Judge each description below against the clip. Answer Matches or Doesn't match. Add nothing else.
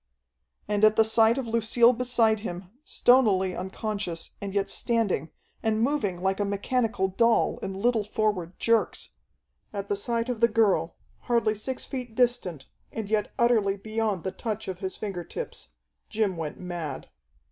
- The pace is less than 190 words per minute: Matches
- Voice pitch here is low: Doesn't match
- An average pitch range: Matches